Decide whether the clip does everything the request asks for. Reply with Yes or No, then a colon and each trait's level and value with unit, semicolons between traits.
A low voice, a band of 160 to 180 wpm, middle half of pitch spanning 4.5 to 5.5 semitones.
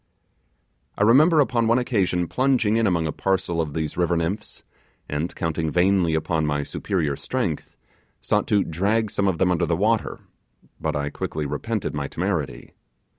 Yes: very low, 90 Hz; average, 165 wpm; average, 4.9 semitones